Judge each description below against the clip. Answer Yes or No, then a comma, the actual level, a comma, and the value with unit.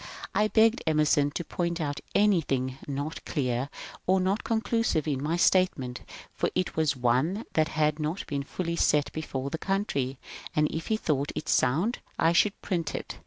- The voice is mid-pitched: Yes, medium, 155 Hz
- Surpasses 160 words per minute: Yes, average, 170 wpm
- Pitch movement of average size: Yes, average, 4.7 semitones